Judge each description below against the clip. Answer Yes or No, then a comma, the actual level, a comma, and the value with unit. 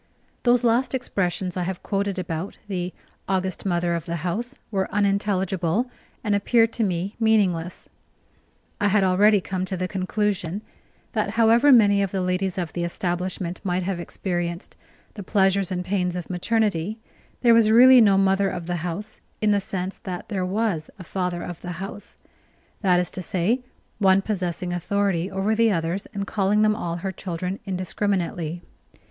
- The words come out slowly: No, average, 165 wpm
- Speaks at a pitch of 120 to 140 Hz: No, high, 190 Hz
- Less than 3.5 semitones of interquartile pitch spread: Yes, average, 2.7 semitones